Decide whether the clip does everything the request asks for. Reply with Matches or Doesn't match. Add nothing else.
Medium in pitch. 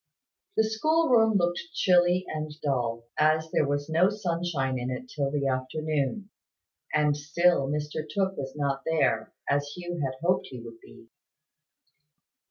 Matches